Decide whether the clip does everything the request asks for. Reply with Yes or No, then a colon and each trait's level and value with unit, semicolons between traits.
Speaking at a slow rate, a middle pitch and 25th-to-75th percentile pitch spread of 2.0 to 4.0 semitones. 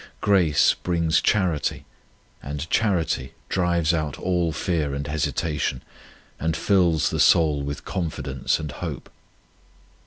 No: slow, 115 wpm; very low, 80 Hz; average, 3.0 semitones